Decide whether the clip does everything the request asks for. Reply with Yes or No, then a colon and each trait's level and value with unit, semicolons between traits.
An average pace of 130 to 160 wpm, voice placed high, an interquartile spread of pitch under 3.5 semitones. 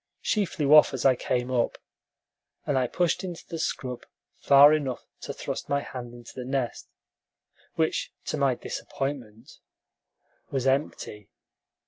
No: average, 140 wpm; low, 135 Hz; average, 2.9 semitones